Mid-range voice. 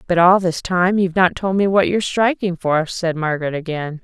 Yes: medium, 180 Hz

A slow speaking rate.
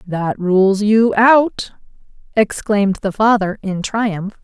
Yes: slow, 120 wpm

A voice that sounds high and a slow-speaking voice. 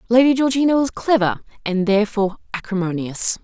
Yes: high, 215 Hz; slow, 120 wpm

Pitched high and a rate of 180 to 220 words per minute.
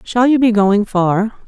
Yes: high, 215 Hz; fast, 205 wpm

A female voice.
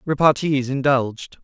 No: male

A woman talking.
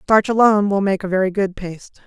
Yes: female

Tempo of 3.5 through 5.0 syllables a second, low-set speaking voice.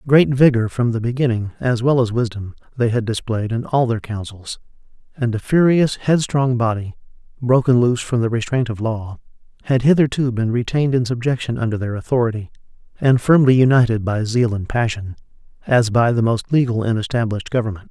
No: 5.6 syllables/s; low, 120 Hz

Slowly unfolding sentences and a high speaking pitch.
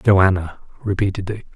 No: slow, 115 wpm; very low, 95 Hz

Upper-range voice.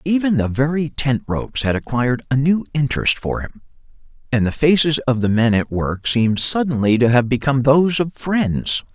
No: low, 135 Hz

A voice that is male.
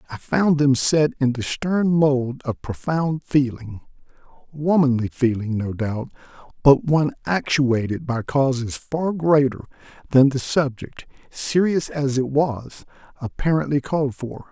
Yes: male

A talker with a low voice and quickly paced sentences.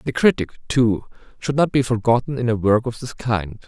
Yes: low, 120 Hz; fast, 215 wpm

